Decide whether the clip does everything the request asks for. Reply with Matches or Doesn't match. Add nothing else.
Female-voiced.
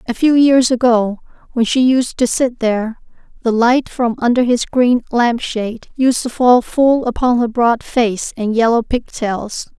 Matches